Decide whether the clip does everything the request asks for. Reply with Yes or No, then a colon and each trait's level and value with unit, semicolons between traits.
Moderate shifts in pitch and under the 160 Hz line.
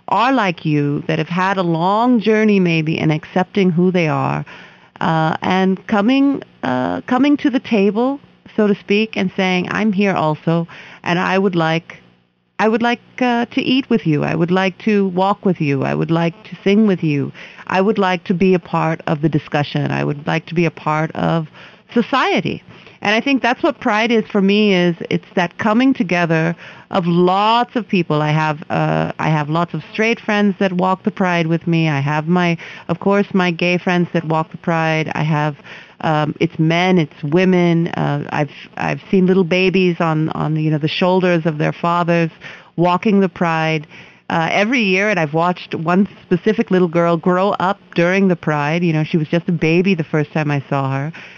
No: average, 3.9 semitones; medium, 180 Hz